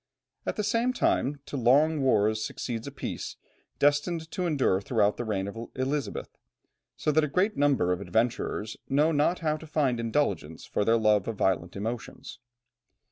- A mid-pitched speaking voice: No, low, 130 Hz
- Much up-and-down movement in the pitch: Yes, wide, 5.8 semitones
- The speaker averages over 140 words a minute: Yes, average, 170 wpm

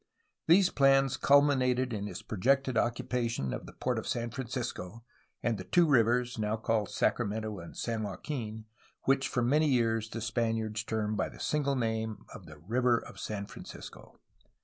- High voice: No, low, 115 Hz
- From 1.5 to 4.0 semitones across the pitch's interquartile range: Yes, average, 3.1 semitones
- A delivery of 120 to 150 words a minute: No, average, 165 wpm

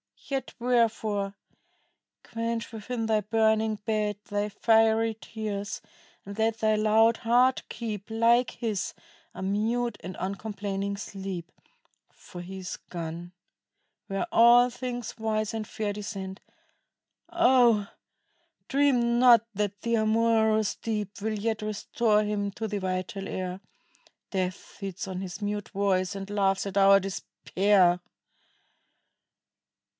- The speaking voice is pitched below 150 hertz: No, high, 210 Hz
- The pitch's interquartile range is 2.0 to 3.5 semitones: Yes, narrow, 2.5 semitones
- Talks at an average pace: No, slow, 120 wpm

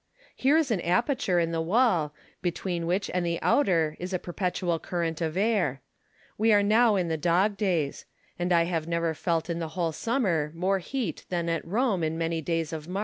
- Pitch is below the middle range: No, medium, 175 Hz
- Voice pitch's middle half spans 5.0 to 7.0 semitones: No, average, 3.2 semitones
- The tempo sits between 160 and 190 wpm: No, fast, 205 wpm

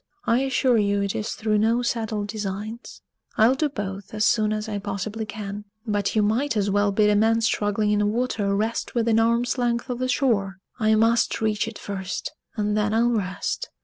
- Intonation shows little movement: Yes, narrow, 2.0 semitones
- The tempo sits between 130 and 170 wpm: No, average, 200 wpm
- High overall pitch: Yes, high, 215 Hz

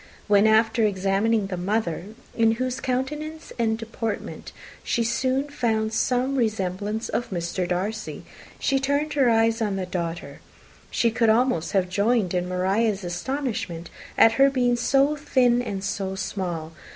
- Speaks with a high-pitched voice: Yes, high, 220 Hz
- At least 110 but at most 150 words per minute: Yes, average, 145 wpm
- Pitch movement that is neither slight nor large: Yes, average, 4.5 semitones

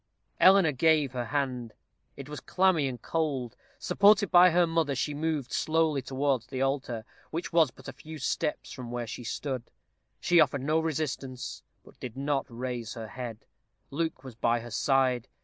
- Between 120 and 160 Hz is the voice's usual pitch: Yes, low, 135 Hz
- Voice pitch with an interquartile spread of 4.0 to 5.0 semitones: Yes, average, 4.3 semitones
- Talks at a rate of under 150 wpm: No, average, 170 wpm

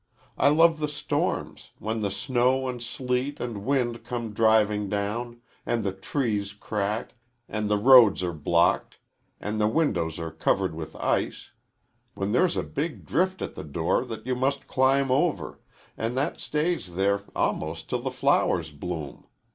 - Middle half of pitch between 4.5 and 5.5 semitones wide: Yes, average, 4.8 semitones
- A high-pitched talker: No, low, 115 Hz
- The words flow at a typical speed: Yes, average, 160 wpm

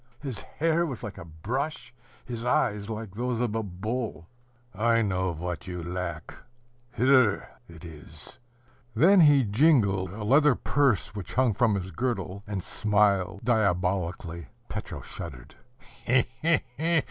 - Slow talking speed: Yes, slow, 130 wpm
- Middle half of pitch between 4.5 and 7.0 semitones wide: Yes, average, 5.2 semitones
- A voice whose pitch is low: Yes, low, 105 Hz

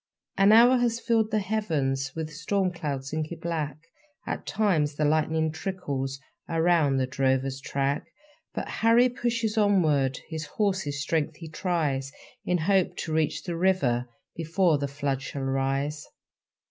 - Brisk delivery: No, average, 145 wpm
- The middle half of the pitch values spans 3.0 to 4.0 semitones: No, wide, 5.4 semitones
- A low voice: No, medium, 155 Hz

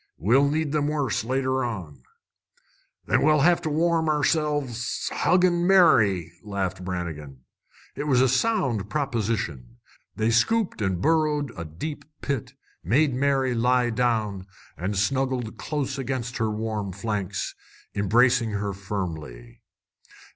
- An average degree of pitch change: No, wide, 6.6 semitones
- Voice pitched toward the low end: Yes, low, 120 Hz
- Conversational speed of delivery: No, slow, 125 wpm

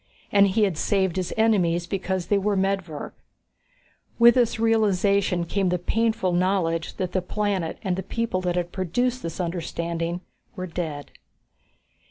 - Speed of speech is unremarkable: Yes, average, 150 wpm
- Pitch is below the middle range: No, medium, 185 Hz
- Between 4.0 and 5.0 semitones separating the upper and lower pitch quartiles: No, average, 2.8 semitones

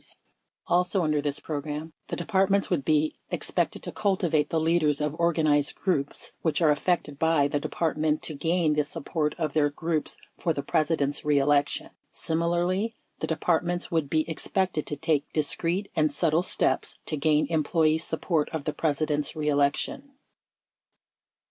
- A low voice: No, medium, 155 Hz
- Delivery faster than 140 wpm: Yes, average, 155 wpm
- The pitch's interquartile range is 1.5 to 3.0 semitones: Yes, narrow, 2.4 semitones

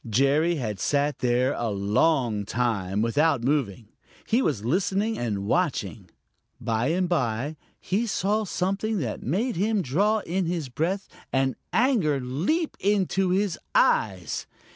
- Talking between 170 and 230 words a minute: No, slow, 135 wpm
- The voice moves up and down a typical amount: No, wide, 8.4 semitones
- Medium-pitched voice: Yes, medium, 150 Hz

